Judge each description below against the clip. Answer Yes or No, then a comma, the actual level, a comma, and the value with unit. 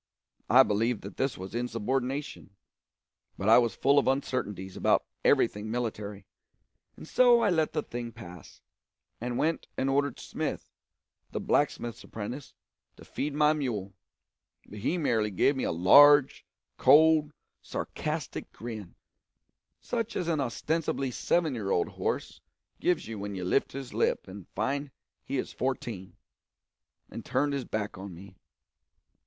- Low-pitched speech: Yes, low, 125 Hz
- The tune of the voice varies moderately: No, wide, 5.7 semitones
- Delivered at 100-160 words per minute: Yes, average, 145 wpm